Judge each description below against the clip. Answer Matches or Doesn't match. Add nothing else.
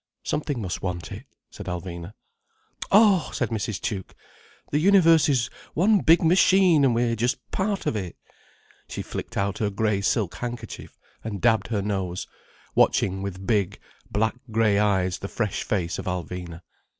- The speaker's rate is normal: Matches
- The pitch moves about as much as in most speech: Doesn't match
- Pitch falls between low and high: Doesn't match